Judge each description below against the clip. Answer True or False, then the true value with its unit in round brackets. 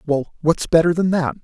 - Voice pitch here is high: False (160 Hz)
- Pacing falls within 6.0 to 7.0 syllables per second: False (5.1 syllables/s)